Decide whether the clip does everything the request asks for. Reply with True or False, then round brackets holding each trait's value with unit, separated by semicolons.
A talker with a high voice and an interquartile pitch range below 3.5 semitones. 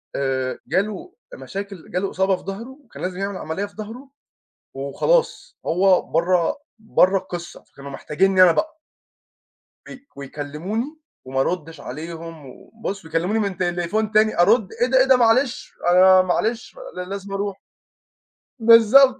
False (195 Hz; 4.7 semitones)